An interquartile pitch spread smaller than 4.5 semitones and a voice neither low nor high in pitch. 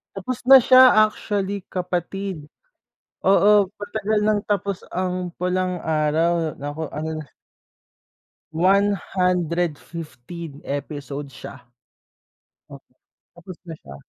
Yes: average, 3.9 semitones; medium, 180 Hz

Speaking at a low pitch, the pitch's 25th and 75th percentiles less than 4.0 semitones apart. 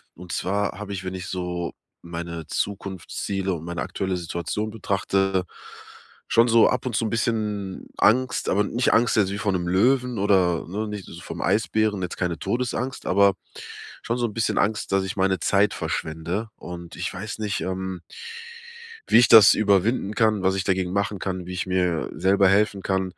Yes: very low, 95 Hz; narrow, 2.6 semitones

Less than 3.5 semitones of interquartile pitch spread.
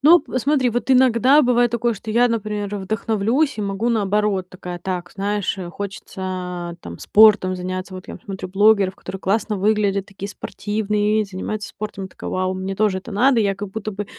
Yes: average, 2.7 semitones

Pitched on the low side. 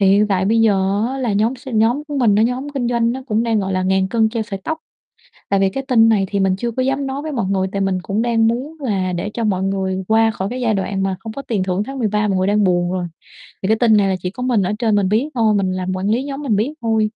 No: high, 215 Hz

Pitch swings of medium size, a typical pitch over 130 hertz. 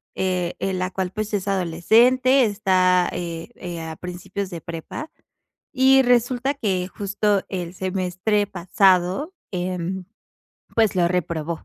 Yes: average, 3.1 semitones; medium, 185 Hz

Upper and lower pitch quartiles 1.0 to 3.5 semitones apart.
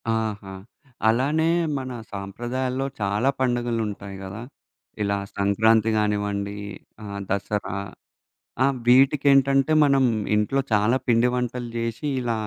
No: average, 4.2 semitones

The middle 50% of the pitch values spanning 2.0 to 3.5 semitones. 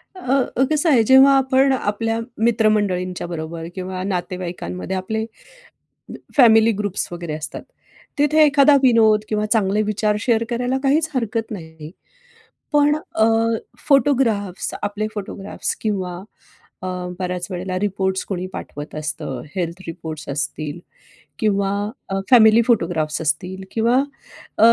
No: average, 4.5 semitones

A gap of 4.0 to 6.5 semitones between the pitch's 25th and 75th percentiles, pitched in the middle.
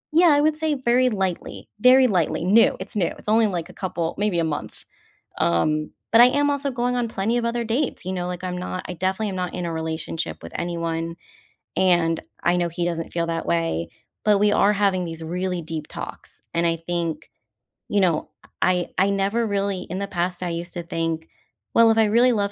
Yes: average, 4.6 semitones; medium, 180 Hz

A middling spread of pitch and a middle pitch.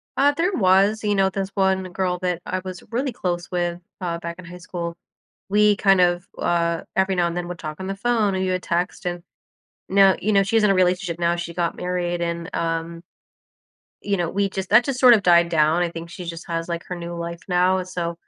No: narrow, 2.2 semitones; medium, 180 Hz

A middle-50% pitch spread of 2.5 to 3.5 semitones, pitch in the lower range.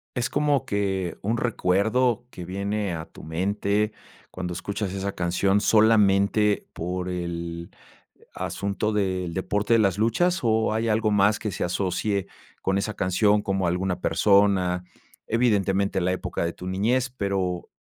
Yes: average, 2.8 semitones; low, 100 Hz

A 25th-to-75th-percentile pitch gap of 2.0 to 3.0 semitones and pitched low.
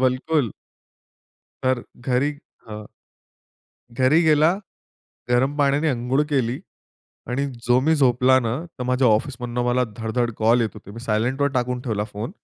Yes: narrow, 2.6 semitones; low, 125 Hz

